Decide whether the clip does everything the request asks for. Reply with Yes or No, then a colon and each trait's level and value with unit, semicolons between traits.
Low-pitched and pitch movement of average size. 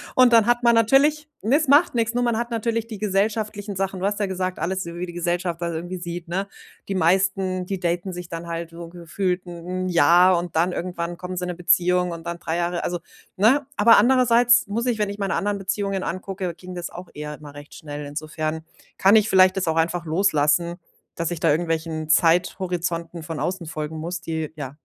No: medium, 180 Hz; average, 3.1 semitones